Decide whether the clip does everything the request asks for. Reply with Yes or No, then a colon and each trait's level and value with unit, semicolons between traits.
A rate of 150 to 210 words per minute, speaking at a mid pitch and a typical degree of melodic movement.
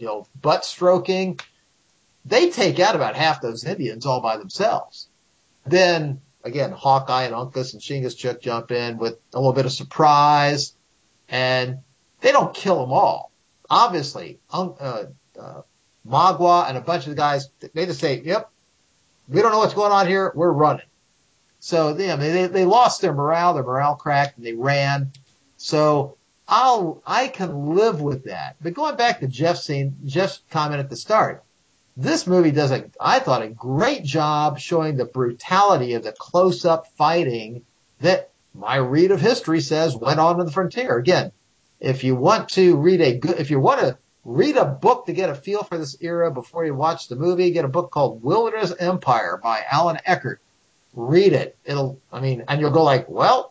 Yes: average, 185 wpm; medium, 150 Hz; average, 5.0 semitones